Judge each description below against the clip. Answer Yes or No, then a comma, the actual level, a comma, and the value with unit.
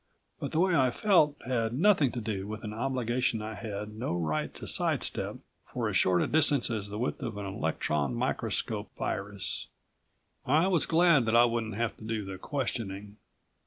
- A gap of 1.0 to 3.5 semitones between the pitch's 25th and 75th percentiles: No, average, 4.6 semitones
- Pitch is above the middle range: No, low, 115 Hz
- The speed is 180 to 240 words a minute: Yes, average, 185 wpm